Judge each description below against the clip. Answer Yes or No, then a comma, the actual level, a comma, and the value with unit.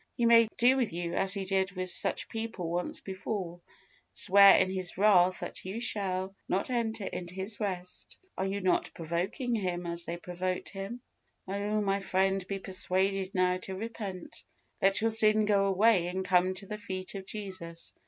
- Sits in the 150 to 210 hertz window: Yes, high, 190 Hz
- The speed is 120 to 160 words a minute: No, average, 180 wpm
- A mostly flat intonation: Yes, narrow, 2.2 semitones